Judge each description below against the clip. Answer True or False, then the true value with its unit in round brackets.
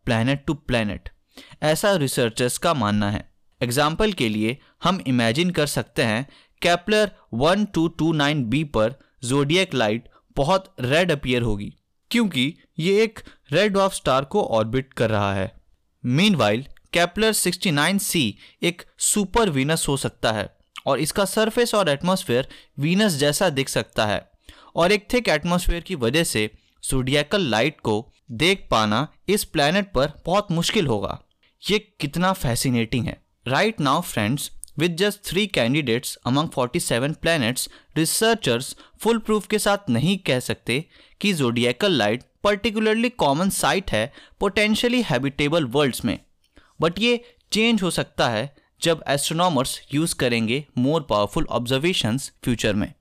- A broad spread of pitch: True (7.5 semitones)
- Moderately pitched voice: True (150 Hz)